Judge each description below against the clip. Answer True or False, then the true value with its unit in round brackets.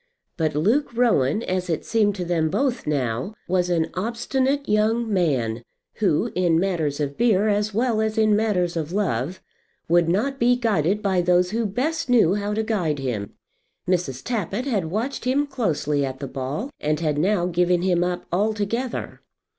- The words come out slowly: False (170 wpm)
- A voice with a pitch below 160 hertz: False (185 Hz)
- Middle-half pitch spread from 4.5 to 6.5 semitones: True (5.6 semitones)